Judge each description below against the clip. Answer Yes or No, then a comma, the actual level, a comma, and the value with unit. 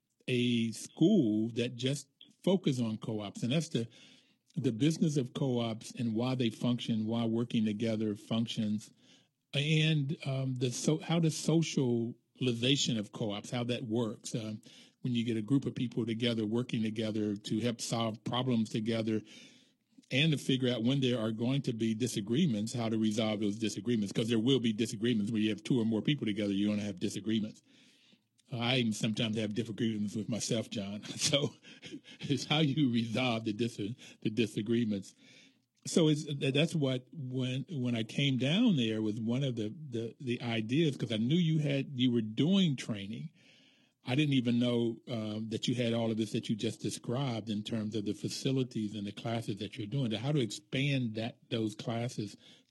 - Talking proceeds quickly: No, average, 180 wpm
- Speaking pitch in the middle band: No, low, 120 Hz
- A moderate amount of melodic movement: Yes, average, 3.4 semitones